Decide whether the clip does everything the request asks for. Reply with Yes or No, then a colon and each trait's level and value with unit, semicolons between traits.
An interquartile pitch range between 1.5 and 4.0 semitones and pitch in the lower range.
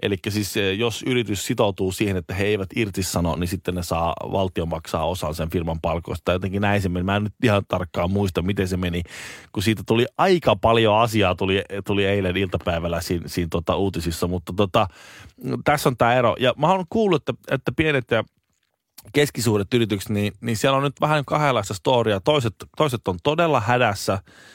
No: average, 4.5 semitones; low, 100 Hz